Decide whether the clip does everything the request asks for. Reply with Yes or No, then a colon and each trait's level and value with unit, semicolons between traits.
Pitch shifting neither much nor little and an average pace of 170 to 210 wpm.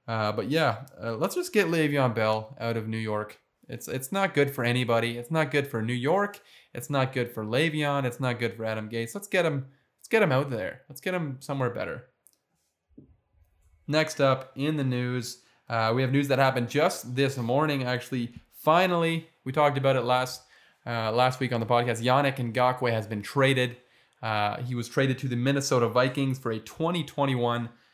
Yes: average, 3.3 semitones; average, 200 wpm